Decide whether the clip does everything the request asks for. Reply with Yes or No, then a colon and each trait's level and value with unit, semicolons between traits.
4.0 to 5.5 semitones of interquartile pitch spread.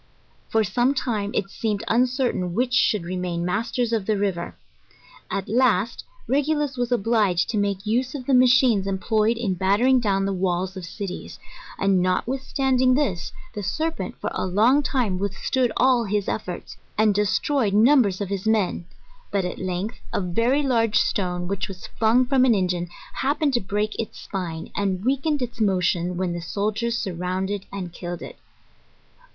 Yes: average, 4.8 semitones